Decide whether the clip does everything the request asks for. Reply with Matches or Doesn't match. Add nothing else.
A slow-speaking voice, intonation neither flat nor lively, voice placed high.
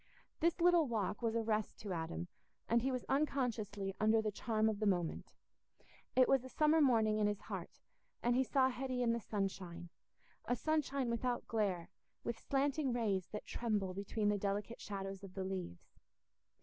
Doesn't match